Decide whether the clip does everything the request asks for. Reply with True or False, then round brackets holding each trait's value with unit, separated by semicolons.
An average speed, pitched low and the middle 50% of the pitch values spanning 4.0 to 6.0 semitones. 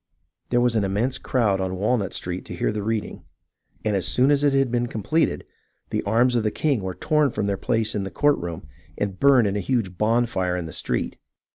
False (225 wpm; 110 Hz; 4.4 semitones)